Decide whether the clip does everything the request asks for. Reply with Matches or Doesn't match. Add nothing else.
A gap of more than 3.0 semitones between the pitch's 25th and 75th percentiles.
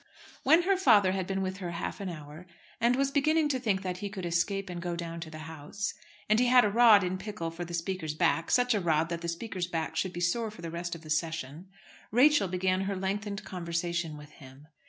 Matches